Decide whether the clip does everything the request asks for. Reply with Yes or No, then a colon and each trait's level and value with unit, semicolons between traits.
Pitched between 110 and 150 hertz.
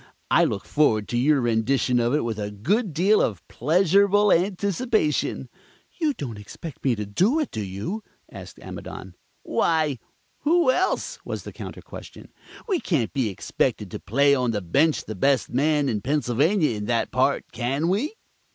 Yes: medium, 140 Hz